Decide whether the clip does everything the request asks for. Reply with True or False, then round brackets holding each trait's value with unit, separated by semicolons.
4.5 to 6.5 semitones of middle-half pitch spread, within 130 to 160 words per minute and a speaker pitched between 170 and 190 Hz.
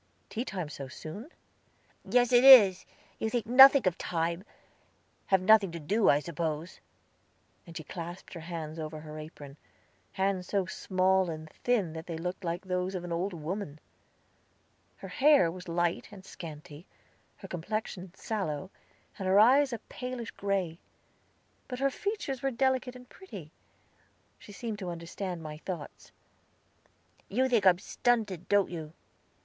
True (5.1 semitones; 155 wpm; 185 Hz)